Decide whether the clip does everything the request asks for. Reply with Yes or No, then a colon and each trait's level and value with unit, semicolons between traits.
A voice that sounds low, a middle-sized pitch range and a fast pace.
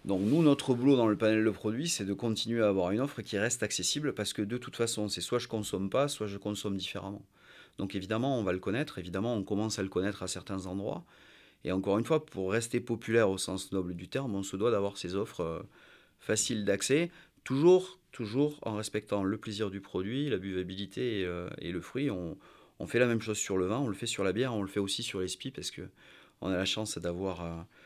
Yes: low, 105 Hz; average, 3.5 semitones; fast, 245 wpm